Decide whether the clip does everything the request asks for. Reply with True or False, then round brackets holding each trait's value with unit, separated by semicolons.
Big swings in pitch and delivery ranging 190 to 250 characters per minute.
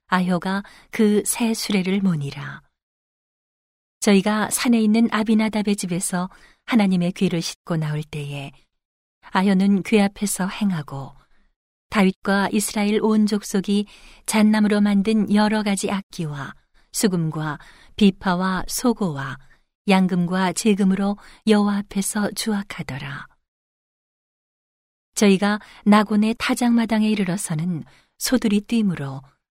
False (2.8 semitones; 245 characters per minute)